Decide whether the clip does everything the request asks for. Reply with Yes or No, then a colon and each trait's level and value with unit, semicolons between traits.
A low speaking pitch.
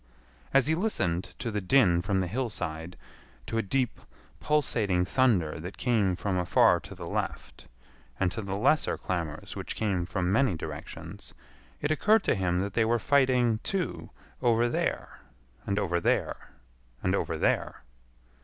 Yes: low, 100 Hz